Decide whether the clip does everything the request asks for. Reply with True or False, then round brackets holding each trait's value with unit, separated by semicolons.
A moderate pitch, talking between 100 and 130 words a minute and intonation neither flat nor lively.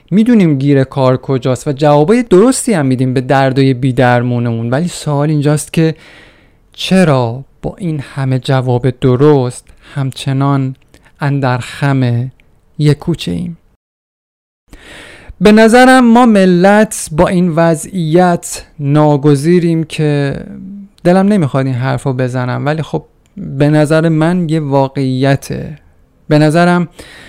True (145 Hz; 115 wpm; 4.7 semitones)